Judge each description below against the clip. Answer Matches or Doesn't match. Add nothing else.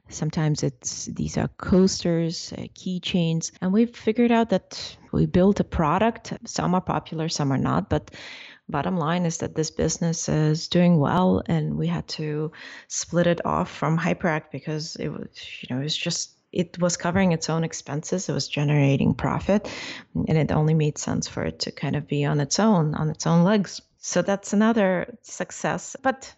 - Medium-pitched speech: Matches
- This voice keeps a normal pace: Matches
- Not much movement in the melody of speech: Doesn't match